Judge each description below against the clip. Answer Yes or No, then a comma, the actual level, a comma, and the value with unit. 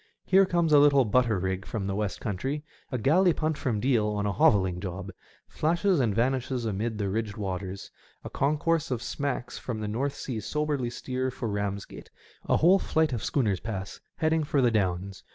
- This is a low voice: Yes, low, 120 Hz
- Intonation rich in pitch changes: Yes, wide, 6.0 semitones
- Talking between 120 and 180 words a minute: No, average, 190 wpm